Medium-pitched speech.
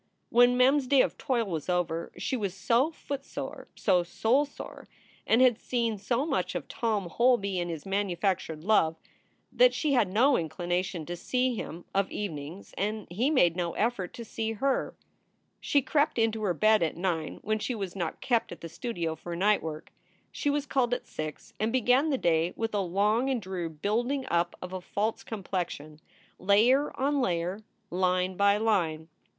No: high, 205 Hz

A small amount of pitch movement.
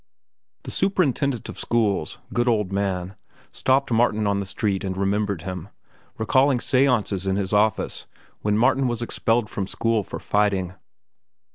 No: average, 3.7 semitones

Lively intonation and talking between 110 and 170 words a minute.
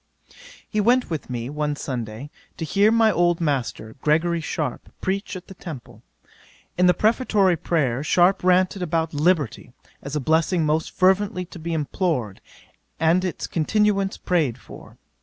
No: average, 4.1 semitones; average, 150 wpm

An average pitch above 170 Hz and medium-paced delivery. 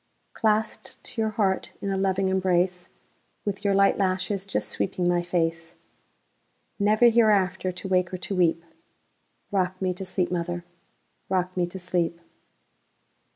No: medium, 185 Hz; slow, 125 wpm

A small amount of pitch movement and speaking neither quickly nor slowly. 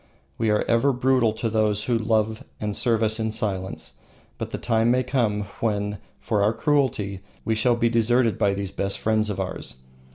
Yes: narrow, 2.1 semitones; average, 190 wpm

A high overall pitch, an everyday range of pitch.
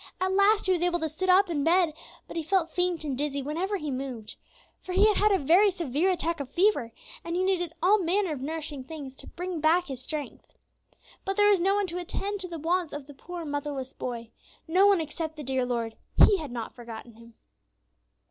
Yes: very high, 330 Hz; average, 4.9 semitones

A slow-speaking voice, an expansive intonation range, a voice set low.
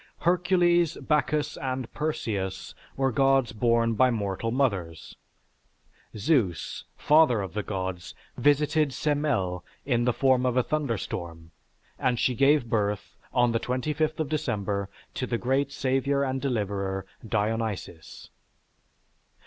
Yes: slow, 120 wpm; wide, 5.7 semitones; low, 125 Hz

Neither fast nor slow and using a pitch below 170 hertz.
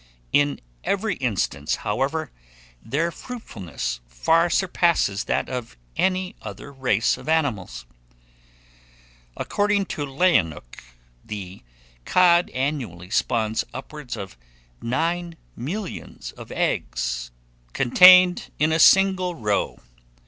No: slow, 100 wpm; medium, 140 Hz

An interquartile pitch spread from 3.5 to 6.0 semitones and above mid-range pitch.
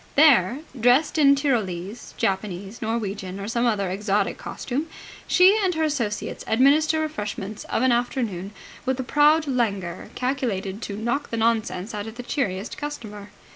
Yes: wide, 5.6 semitones; high, 230 Hz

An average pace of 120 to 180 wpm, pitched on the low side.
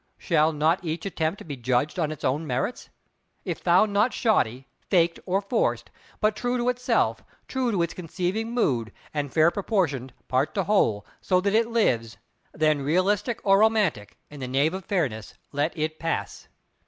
No: average, 165 wpm; medium, 170 Hz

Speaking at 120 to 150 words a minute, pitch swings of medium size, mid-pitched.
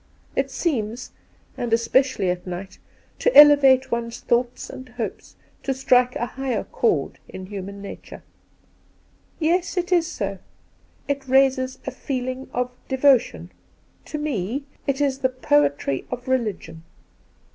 No: average, 140 wpm; average, 3.5 semitones; very high, 255 Hz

